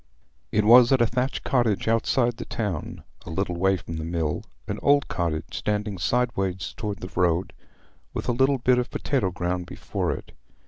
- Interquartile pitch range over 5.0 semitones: Yes, wide, 5.6 semitones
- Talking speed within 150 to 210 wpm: Yes, average, 175 wpm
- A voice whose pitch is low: Yes, low, 105 Hz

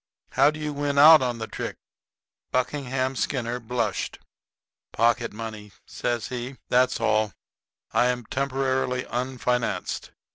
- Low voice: Yes, low, 125 Hz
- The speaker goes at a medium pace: No, slow, 120 wpm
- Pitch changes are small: Yes, narrow, 2.1 semitones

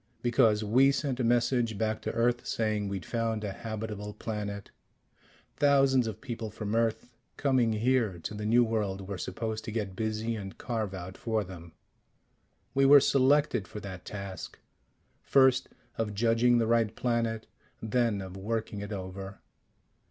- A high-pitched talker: No, low, 110 Hz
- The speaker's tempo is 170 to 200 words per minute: No, average, 155 wpm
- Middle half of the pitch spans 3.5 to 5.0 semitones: No, average, 2.8 semitones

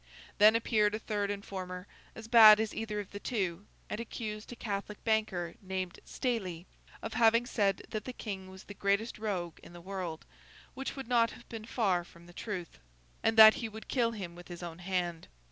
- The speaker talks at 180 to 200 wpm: Yes, average, 195 wpm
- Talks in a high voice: Yes, high, 205 Hz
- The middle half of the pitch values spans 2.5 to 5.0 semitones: Yes, average, 3.4 semitones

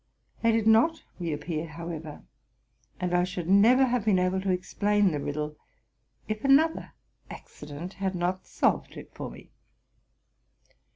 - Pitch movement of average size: Yes, average, 4.6 semitones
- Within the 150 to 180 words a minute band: No, average, 140 wpm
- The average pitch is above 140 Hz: Yes, medium, 185 Hz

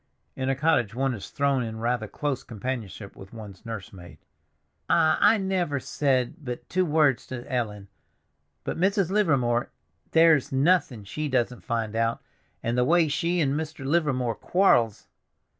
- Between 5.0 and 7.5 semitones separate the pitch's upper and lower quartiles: Yes, wide, 5.5 semitones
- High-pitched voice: No, low, 130 Hz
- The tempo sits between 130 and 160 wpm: Yes, average, 150 wpm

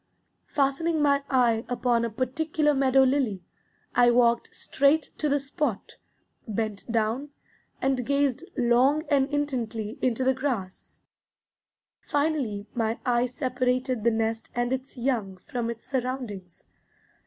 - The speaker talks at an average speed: No, slow, 125 wpm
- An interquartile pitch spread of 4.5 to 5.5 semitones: No, average, 3.2 semitones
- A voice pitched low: No, very high, 255 Hz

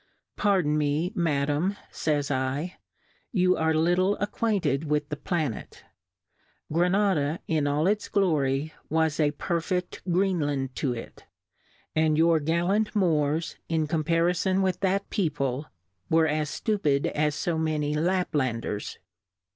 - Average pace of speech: No, slow, 130 wpm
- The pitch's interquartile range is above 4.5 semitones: No, average, 3.6 semitones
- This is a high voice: No, medium, 160 Hz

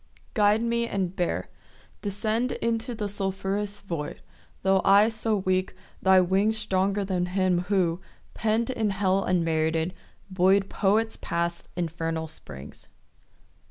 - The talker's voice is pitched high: Yes, high, 195 Hz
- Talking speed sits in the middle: No, slow, 125 wpm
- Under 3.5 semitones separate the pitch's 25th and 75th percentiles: Yes, average, 3.0 semitones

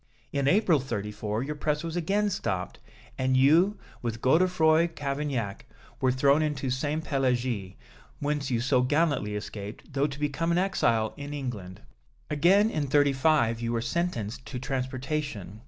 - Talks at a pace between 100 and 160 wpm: Yes, average, 145 wpm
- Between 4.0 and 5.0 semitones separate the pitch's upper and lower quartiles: Yes, average, 4.5 semitones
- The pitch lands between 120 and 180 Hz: Yes, medium, 140 Hz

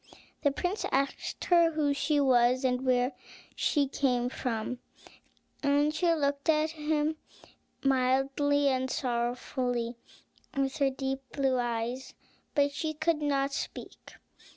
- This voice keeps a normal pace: No, slow, 125 wpm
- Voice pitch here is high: Yes, very high, 275 Hz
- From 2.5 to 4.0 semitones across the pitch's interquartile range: Yes, average, 2.8 semitones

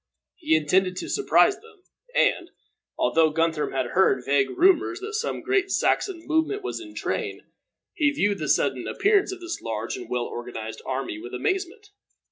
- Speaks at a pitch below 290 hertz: No, very high, 295 Hz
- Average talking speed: Yes, average, 165 wpm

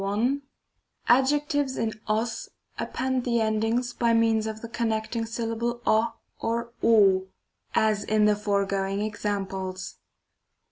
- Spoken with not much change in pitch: Yes, narrow, 2.2 semitones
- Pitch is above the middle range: Yes, high, 220 Hz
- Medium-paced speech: No, slow, 125 wpm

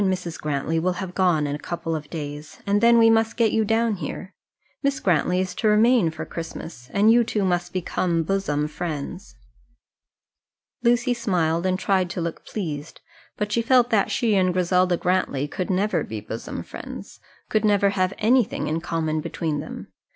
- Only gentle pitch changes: No, average, 4.6 semitones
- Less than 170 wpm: No, average, 180 wpm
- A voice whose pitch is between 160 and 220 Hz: Yes, medium, 185 Hz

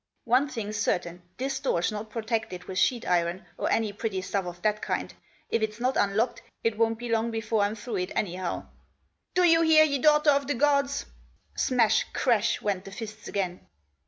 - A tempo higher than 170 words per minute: Yes, average, 190 wpm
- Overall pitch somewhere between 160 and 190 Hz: No, high, 220 Hz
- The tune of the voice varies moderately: Yes, average, 4.2 semitones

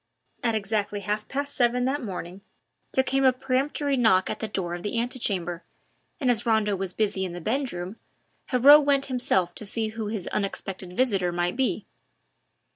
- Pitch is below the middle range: No, high, 220 Hz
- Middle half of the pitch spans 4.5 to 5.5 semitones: Yes, average, 5.1 semitones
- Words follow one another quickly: No, average, 175 wpm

